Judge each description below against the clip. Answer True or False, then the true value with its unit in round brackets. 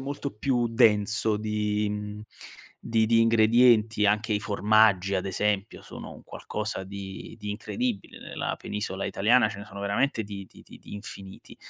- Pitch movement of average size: False (1.8 semitones)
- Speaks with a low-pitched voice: True (105 Hz)